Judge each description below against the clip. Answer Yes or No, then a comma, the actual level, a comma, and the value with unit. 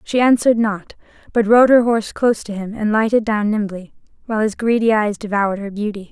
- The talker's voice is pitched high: Yes, high, 215 Hz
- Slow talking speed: No, fast, 205 wpm